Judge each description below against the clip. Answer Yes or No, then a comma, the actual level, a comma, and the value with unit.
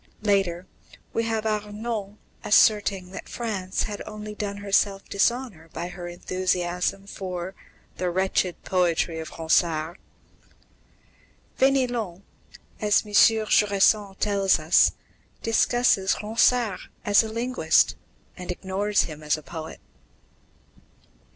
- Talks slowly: Yes, slow, 105 wpm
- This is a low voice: No, high, 195 Hz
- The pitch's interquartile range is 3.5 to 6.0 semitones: No, average, 3.0 semitones